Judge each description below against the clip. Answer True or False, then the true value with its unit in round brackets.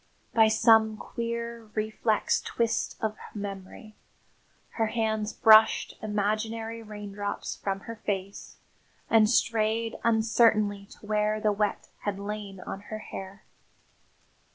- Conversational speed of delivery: False (110 wpm)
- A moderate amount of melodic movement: False (1.4 semitones)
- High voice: True (215 Hz)